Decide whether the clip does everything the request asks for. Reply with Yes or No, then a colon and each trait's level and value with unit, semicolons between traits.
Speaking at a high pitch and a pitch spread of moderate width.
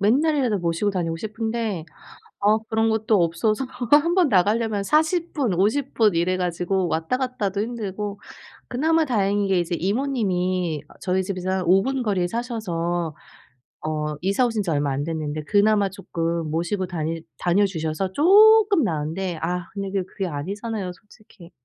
Yes: high, 195 Hz; average, 4.6 semitones